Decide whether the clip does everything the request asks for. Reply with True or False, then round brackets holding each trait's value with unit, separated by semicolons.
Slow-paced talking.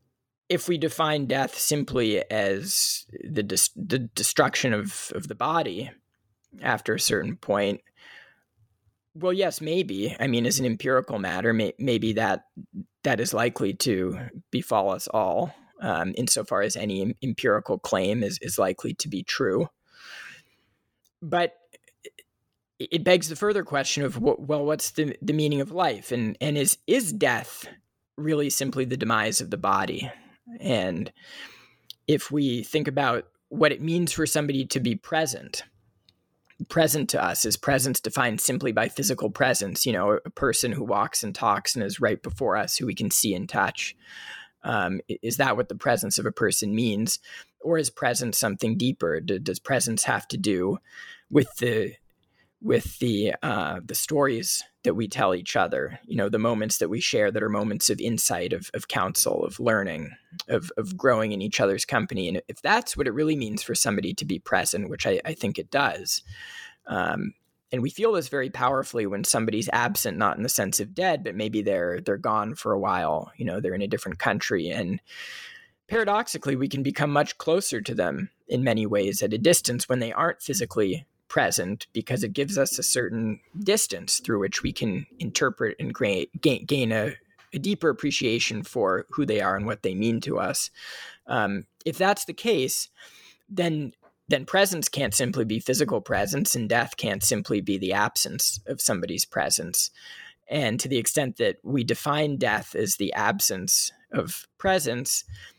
False (175 wpm)